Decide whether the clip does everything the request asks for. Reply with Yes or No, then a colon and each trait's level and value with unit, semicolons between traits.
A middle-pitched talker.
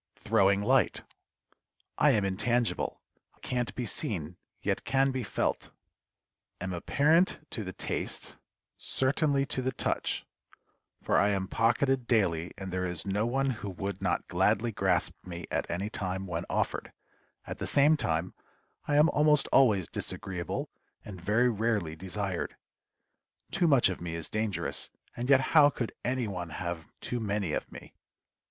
No: low, 105 Hz